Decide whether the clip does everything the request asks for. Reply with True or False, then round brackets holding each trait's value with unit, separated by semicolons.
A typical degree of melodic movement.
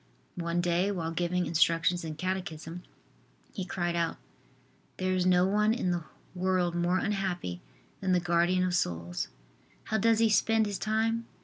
False (2.2 semitones)